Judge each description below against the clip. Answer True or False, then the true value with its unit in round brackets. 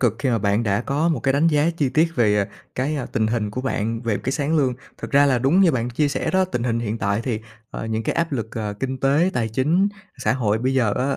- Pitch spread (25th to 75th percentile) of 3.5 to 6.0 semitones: True (4.4 semitones)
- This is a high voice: False (130 Hz)